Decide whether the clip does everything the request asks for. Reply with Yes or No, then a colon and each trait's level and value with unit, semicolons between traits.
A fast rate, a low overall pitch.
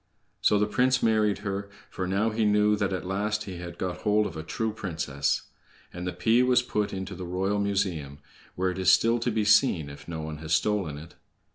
Yes: fast, 220 wpm; low, 100 Hz